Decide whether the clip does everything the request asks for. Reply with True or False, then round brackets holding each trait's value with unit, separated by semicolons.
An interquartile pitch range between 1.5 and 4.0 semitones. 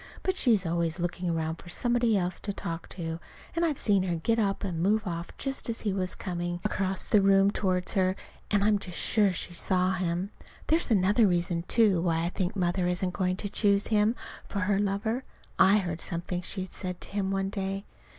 True (2.8 semitones)